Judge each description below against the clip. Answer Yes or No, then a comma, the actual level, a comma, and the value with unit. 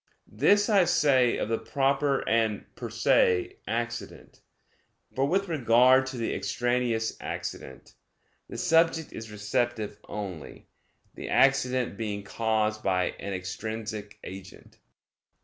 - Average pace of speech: No, slow, 115 wpm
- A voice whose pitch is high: No, low, 120 Hz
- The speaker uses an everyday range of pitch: Yes, average, 4.5 semitones